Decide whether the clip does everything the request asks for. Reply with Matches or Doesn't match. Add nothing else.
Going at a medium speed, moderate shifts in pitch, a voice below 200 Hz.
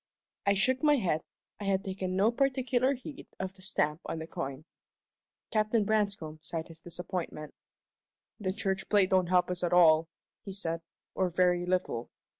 Matches